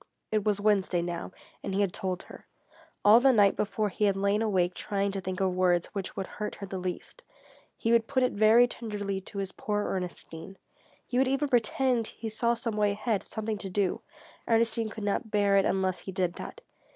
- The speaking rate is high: Yes, fast, 210 wpm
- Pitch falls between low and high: No, high, 205 Hz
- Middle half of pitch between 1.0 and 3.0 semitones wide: Yes, average, 2.7 semitones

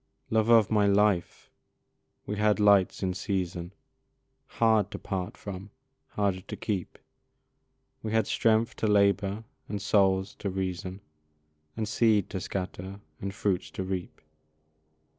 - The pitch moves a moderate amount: No, narrow, 2.0 semitones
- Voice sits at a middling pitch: No, low, 100 Hz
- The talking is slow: Yes, slow, 130 wpm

